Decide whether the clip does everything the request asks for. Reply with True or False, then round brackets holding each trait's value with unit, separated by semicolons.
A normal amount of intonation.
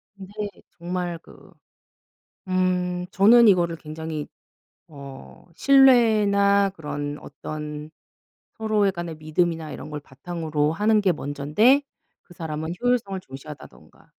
True (4.7 semitones)